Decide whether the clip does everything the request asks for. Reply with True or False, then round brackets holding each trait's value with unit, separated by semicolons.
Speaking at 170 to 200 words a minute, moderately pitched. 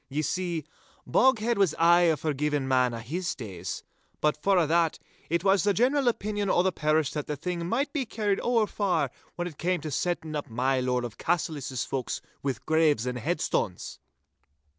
True (185 wpm; 160 Hz)